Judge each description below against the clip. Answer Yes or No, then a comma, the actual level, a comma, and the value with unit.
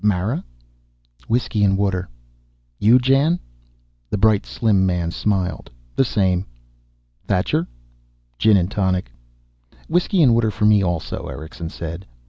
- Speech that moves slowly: Yes, slow, 120 wpm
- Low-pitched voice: Yes, low, 100 Hz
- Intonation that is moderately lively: Yes, average, 3.7 semitones